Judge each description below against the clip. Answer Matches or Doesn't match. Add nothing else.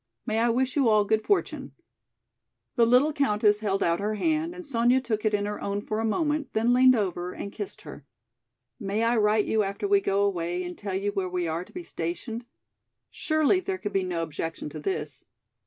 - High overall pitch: Matches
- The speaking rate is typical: Doesn't match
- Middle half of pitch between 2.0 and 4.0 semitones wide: Doesn't match